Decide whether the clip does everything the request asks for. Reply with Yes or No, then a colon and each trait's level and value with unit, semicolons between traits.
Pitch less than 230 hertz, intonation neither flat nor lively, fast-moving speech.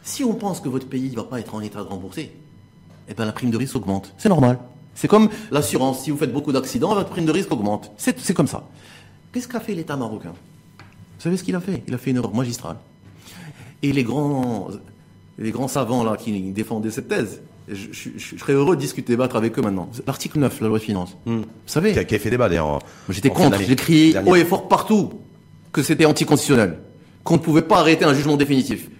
No: low, 135 Hz; wide, 6.1 semitones; fast, 235 wpm